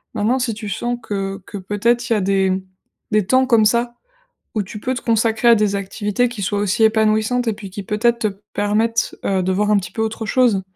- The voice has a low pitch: No, high, 215 Hz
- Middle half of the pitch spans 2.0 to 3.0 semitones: Yes, narrow, 2.6 semitones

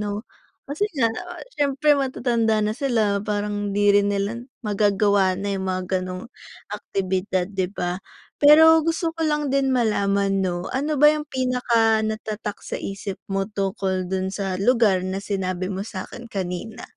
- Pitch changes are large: No, average, 4.2 semitones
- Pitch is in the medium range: No, high, 205 Hz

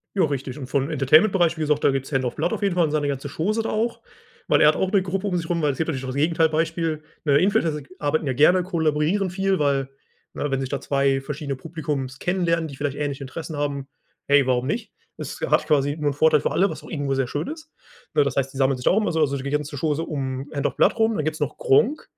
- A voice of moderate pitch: Yes, medium, 150 Hz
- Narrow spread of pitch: No, average, 3.6 semitones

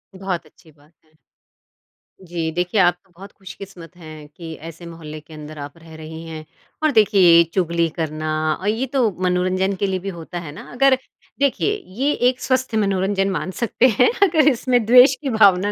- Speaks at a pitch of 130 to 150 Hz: No, medium, 185 Hz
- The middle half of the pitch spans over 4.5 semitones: Yes, average, 5.1 semitones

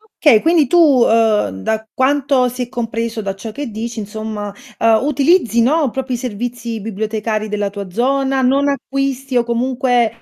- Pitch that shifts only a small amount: No, average, 3.6 semitones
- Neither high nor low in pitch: No, high, 235 Hz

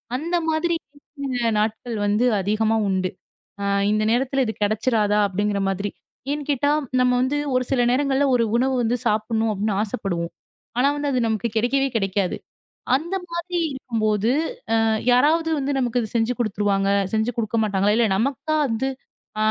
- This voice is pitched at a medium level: No, high, 230 Hz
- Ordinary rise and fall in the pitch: Yes, average, 4.2 semitones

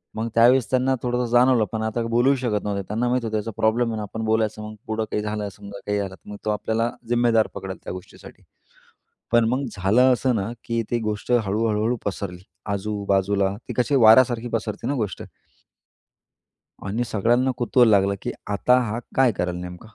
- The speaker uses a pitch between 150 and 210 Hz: No, low, 110 Hz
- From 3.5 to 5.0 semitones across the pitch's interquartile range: No, average, 2.8 semitones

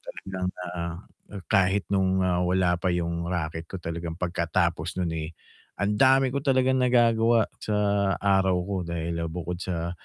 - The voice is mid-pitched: No, very low, 95 Hz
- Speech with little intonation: No, average, 3.1 semitones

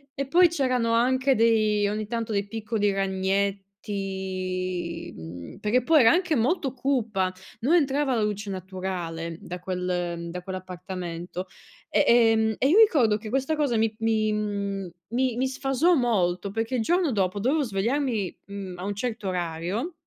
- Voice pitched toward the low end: No, high, 215 Hz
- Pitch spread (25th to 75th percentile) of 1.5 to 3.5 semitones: No, average, 5.3 semitones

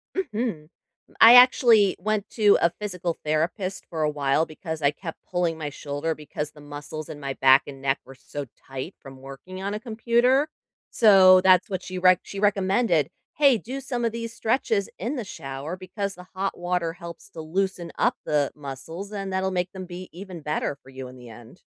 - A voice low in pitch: No, medium, 180 Hz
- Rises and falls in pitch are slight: No, average, 5.2 semitones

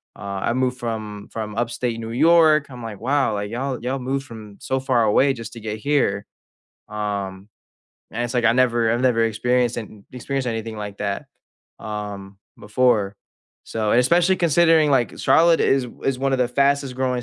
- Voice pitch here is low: Yes, low, 120 Hz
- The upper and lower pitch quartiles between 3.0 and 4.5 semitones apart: Yes, average, 3.8 semitones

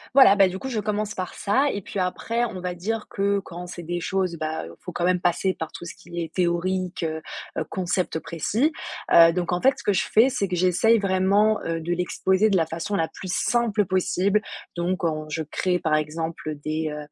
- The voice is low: No, medium, 180 Hz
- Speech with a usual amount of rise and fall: Yes, average, 3.1 semitones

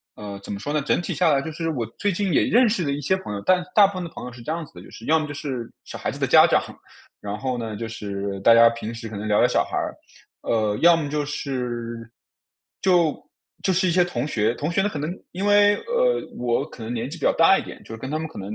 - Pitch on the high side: No, medium, 145 Hz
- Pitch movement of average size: No, wide, 7.1 semitones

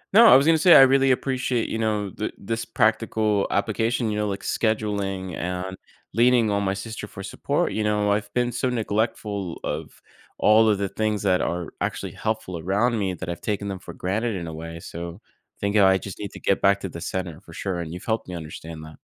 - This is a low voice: Yes, low, 105 Hz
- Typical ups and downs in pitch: Yes, average, 3.2 semitones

